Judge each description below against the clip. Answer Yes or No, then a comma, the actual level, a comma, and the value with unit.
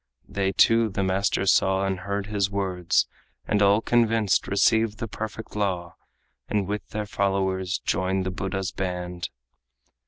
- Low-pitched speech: Yes, low, 100 Hz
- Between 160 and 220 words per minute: No, average, 145 wpm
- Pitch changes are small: Yes, narrow, 1.8 semitones